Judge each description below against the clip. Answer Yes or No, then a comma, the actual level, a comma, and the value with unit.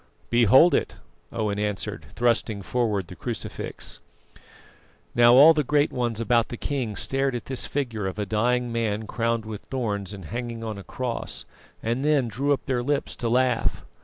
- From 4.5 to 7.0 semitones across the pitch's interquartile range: No, average, 3.2 semitones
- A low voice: Yes, low, 120 Hz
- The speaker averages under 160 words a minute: No, average, 170 wpm